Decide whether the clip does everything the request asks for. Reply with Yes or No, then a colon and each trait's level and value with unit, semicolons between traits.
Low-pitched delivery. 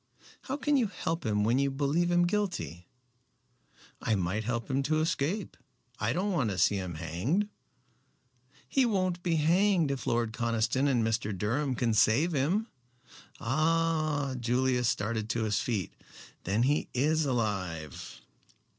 Yes: low, 130 Hz